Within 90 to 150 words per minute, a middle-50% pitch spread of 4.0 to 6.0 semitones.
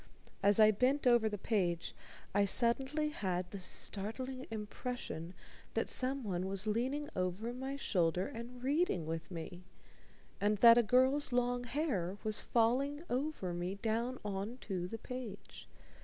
Yes: average, 140 wpm; average, 4.9 semitones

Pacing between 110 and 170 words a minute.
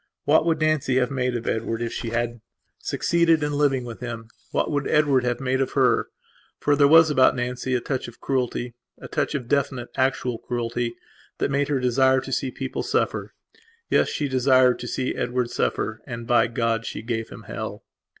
No: average, 190 wpm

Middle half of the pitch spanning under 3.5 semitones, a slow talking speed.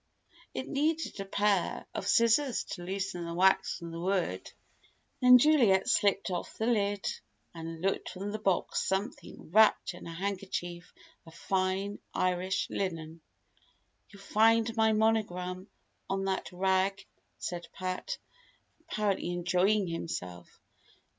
Yes: average, 3.1 semitones; slow, 125 wpm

